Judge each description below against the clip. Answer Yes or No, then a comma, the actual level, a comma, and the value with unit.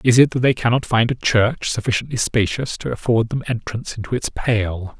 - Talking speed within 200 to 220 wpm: Yes, fast, 205 wpm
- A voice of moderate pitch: No, low, 115 Hz